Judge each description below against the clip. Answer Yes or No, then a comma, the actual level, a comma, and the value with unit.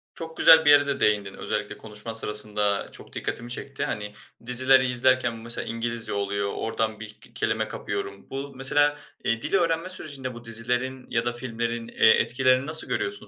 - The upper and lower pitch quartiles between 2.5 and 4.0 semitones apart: Yes, average, 3.5 semitones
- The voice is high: No, low, 120 Hz